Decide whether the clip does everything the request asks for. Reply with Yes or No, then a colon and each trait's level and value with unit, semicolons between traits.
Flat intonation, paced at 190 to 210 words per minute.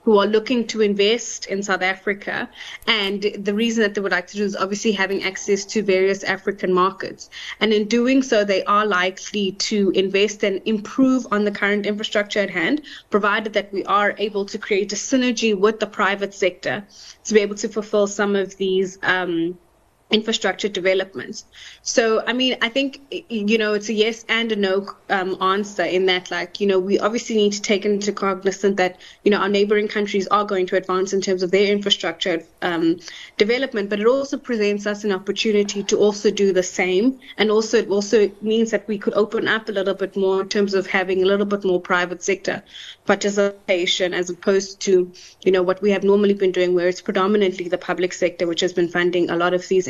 Yes: narrow, 2.1 semitones; fast, 205 wpm